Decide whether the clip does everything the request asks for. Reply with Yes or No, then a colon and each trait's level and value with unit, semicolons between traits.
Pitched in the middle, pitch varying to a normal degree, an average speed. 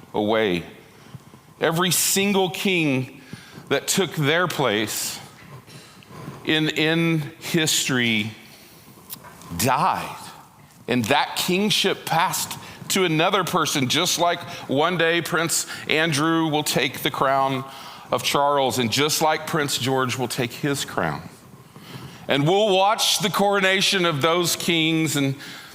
No: medium, 155 Hz; average, 4.2 semitones; slow, 115 wpm